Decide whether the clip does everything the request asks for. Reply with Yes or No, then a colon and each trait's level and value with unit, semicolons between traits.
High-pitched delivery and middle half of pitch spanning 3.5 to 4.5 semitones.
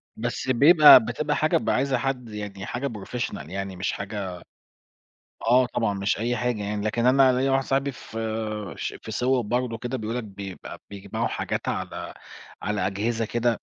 No: low, 115 Hz; average, 3.9 semitones